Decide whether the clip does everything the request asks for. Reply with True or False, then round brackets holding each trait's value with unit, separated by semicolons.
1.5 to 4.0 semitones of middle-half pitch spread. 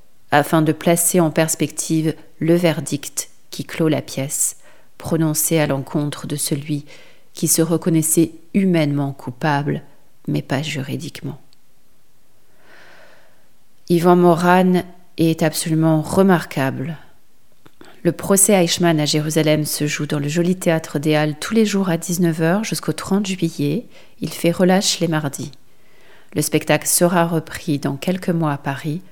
True (2.4 semitones)